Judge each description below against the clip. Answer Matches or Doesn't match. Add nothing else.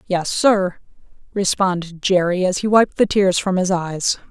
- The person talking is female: Matches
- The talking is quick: Doesn't match